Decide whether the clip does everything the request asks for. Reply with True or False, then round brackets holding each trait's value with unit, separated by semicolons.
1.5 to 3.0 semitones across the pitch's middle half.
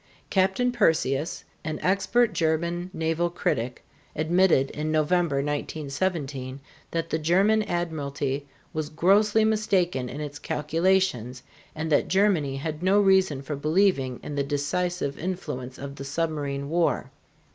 False (4.7 semitones)